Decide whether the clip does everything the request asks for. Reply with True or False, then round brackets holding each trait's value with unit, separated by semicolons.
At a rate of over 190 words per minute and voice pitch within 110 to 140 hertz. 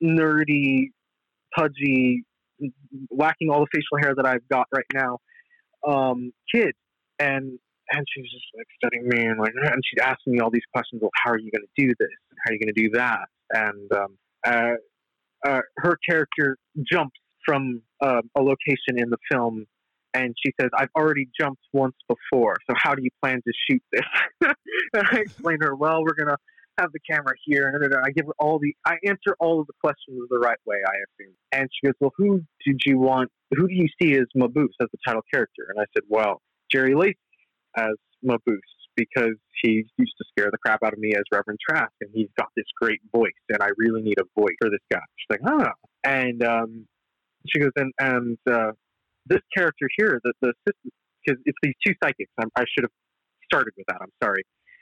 True (205 wpm; 135 Hz)